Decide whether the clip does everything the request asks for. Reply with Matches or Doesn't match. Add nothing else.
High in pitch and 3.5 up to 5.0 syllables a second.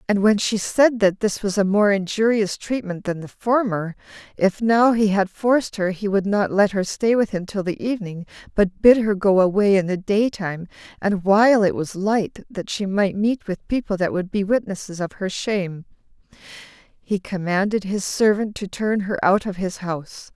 Matches